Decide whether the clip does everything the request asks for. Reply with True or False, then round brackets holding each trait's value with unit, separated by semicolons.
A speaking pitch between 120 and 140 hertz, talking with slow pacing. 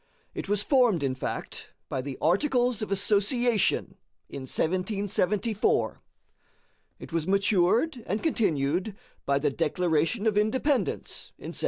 False (200 Hz; 125 wpm)